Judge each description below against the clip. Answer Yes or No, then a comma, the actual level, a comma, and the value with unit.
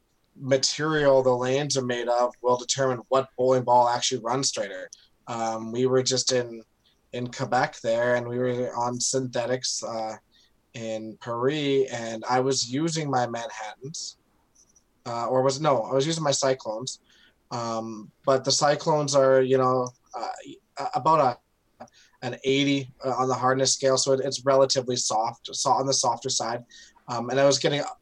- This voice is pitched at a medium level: No, low, 130 Hz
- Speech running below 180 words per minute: Yes, average, 165 wpm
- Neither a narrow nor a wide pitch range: No, narrow, 2.0 semitones